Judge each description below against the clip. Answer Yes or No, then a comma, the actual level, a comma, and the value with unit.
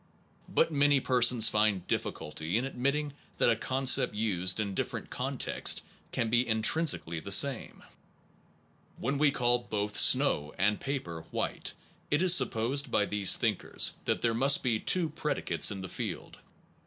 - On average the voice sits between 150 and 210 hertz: No, low, 120 Hz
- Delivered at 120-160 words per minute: Yes, average, 150 wpm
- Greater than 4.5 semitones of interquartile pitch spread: Yes, average, 5.0 semitones